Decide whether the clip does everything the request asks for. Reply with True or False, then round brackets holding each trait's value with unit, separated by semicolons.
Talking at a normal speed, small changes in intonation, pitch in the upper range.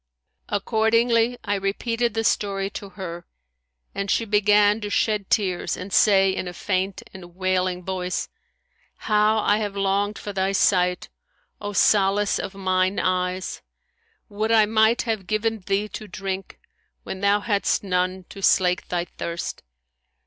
True (145 wpm; 2.1 semitones; 200 Hz)